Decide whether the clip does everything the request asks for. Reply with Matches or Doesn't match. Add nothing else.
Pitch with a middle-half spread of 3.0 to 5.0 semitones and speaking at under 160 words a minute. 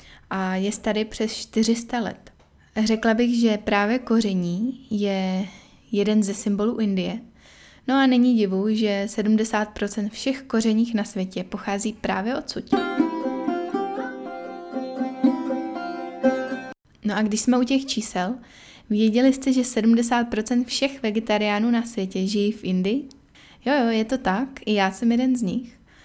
Matches